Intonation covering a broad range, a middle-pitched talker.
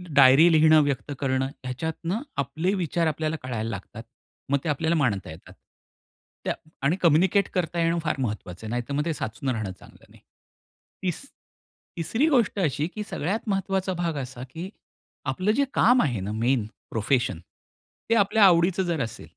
Yes: wide, 5.7 semitones; medium, 155 Hz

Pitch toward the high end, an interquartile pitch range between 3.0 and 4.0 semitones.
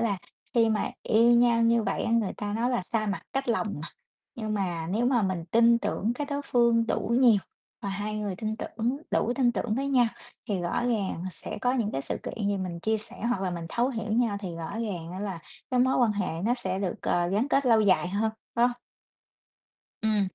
Yes: high, 220 Hz; average, 3.4 semitones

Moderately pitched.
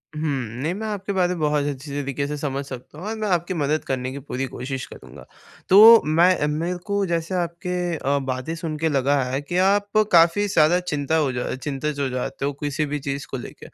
Yes: medium, 150 Hz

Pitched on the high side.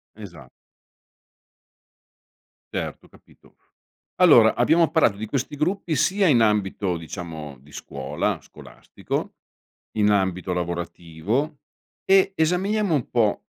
No: low, 110 Hz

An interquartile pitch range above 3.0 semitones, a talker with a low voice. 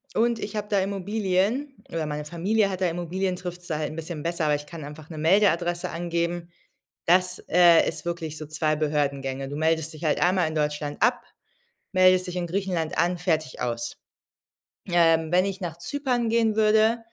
No: average, 3.4 semitones; medium, 175 Hz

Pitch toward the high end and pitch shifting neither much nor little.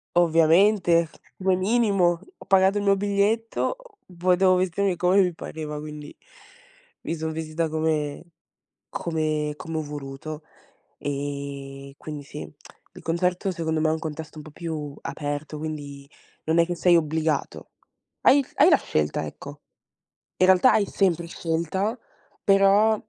No: medium, 165 Hz; average, 3.7 semitones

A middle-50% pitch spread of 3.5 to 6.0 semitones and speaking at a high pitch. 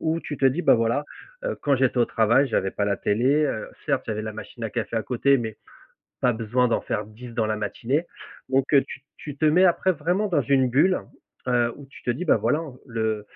No: average, 4.6 semitones; low, 125 Hz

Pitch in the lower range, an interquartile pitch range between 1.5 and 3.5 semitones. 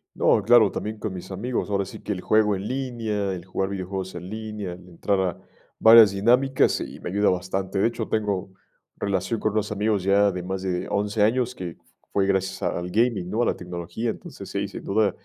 Yes: low, 100 Hz; narrow, 2.6 semitones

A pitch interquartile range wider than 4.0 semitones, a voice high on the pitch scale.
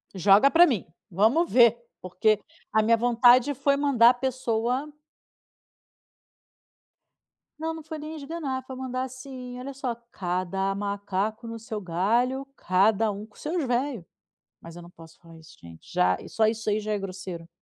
Yes: average, 5.1 semitones; high, 230 Hz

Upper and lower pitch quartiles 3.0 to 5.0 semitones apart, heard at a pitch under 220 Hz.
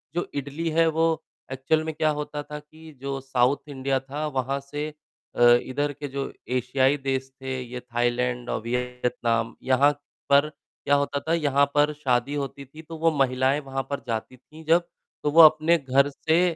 No: narrow, 2.6 semitones; medium, 140 Hz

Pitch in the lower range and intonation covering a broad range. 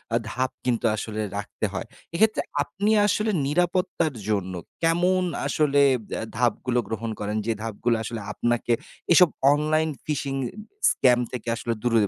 Yes: low, 125 Hz; wide, 6.4 semitones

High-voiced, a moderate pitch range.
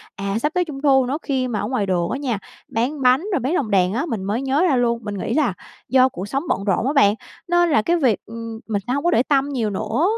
Yes: very high, 250 Hz; average, 5.0 semitones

